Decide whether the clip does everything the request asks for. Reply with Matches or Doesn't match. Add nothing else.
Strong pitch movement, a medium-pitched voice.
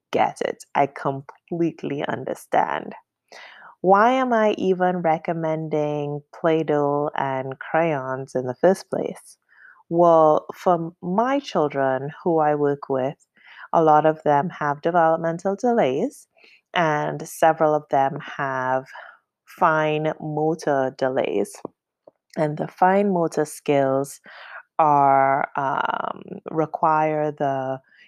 Doesn't match